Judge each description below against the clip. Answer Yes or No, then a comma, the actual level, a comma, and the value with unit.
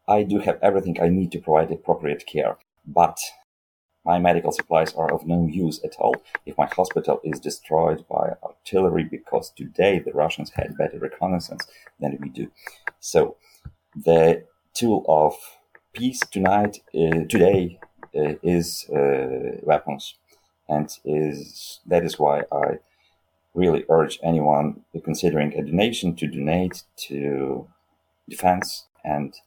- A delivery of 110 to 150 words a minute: Yes, slow, 135 wpm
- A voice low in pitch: Yes, very low, 80 Hz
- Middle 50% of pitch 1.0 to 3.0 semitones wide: Yes, narrow, 2.5 semitones